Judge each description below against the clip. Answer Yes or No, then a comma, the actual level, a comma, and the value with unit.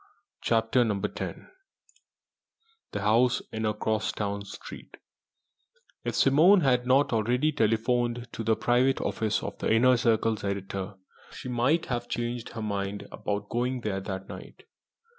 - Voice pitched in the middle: No, low, 115 Hz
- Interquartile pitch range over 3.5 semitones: No, average, 2.9 semitones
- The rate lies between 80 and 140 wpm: Yes, slow, 135 wpm